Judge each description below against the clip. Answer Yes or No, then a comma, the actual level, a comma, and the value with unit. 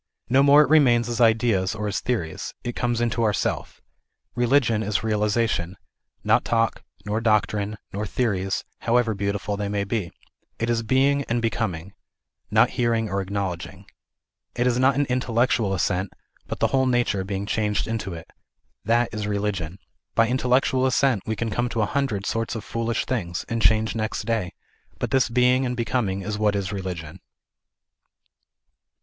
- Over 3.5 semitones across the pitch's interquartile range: No, average, 3.2 semitones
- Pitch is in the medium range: No, low, 110 Hz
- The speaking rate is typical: Yes, average, 165 wpm